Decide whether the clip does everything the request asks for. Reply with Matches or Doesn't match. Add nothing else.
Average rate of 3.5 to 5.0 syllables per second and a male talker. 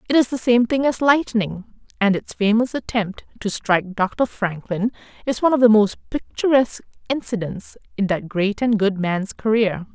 Doesn't match